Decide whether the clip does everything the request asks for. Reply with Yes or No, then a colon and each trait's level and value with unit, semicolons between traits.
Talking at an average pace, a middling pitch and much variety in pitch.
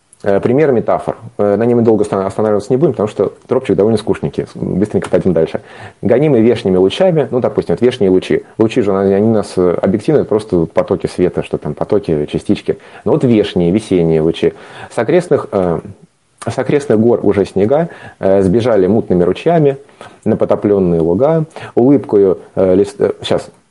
No: average, 145 wpm; low, 105 Hz; wide, 5.7 semitones